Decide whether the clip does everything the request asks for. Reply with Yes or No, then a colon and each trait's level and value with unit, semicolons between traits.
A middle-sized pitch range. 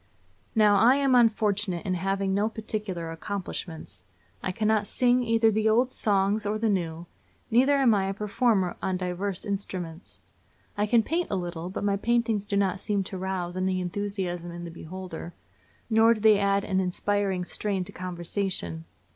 Yes: average, 3.0 semitones